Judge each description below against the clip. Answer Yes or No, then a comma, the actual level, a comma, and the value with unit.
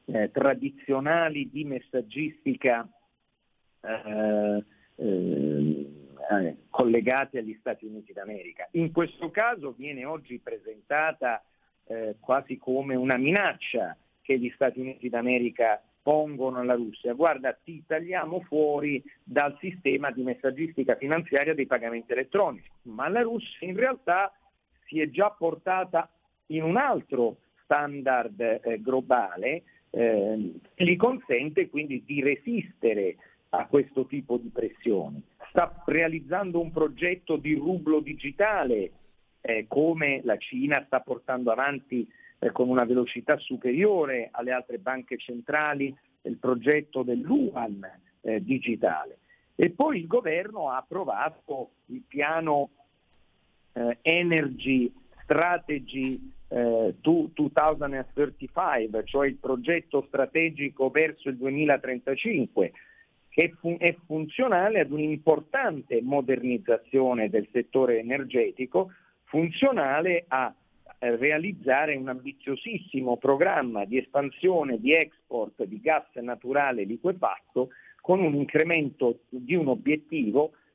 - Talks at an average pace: No, slow, 110 wpm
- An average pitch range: Yes, average, 4.6 semitones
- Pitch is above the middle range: No, medium, 140 Hz